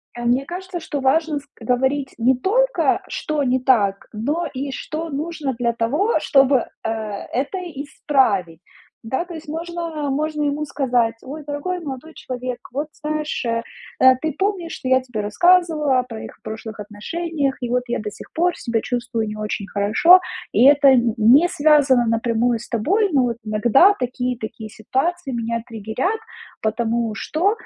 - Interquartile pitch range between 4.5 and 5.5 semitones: Yes, average, 5.0 semitones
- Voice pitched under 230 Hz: No, very high, 265 Hz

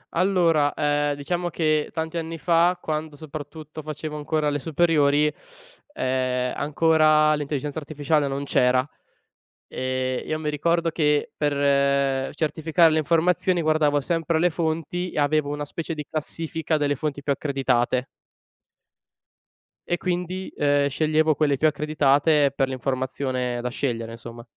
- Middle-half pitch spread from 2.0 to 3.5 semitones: Yes, narrow, 2.4 semitones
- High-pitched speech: No, medium, 150 Hz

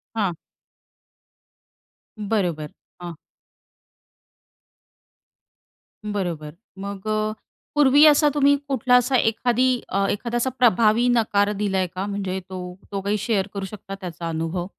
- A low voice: No, high, 205 Hz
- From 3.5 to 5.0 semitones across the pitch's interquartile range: Yes, average, 4.2 semitones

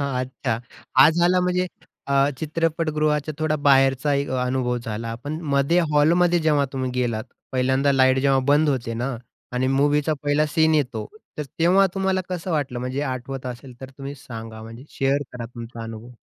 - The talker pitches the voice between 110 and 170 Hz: Yes, low, 135 Hz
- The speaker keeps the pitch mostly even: No, average, 3.3 semitones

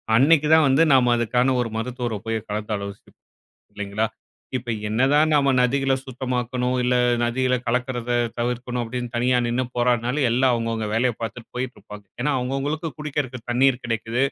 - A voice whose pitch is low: Yes, low, 125 Hz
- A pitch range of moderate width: No, narrow, 2.0 semitones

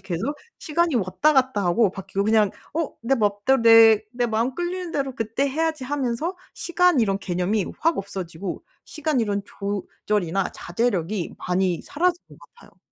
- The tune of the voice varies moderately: No, wide, 6.7 semitones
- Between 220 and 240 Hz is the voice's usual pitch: Yes, high, 225 Hz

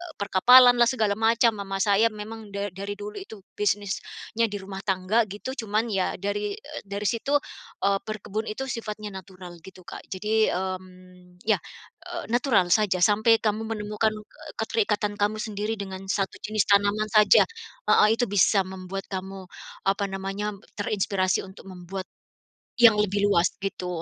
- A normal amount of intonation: No, narrow, 2.1 semitones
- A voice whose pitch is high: Yes, high, 205 Hz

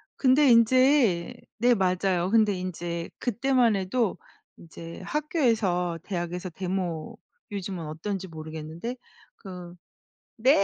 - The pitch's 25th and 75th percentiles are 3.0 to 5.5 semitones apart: Yes, average, 5.2 semitones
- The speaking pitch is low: No, high, 190 Hz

